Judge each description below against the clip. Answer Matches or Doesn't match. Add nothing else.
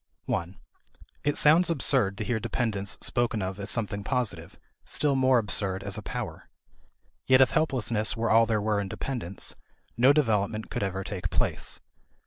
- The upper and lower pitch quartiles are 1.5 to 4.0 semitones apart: Doesn't match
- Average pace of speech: Matches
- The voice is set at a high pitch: Doesn't match